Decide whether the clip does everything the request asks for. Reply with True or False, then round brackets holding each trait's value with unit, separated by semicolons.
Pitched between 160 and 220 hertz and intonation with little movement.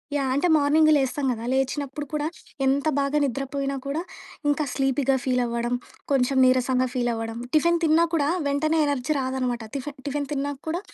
False (275 Hz; 2.2 semitones)